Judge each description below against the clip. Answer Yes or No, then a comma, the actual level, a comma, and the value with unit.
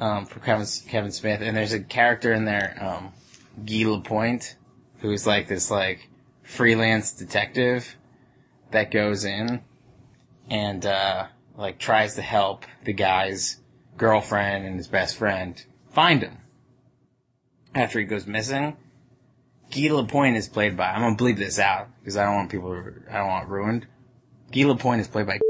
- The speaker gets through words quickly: No, average, 160 wpm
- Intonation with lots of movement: No, average, 3.7 semitones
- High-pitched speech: No, low, 110 Hz